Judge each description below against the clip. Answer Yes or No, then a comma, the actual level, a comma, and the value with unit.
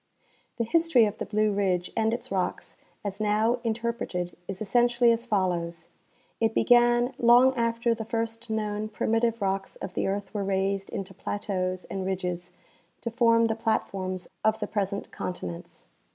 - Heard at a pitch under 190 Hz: No, high, 215 Hz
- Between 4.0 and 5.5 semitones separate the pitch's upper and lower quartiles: No, average, 3.2 semitones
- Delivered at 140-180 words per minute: Yes, average, 160 wpm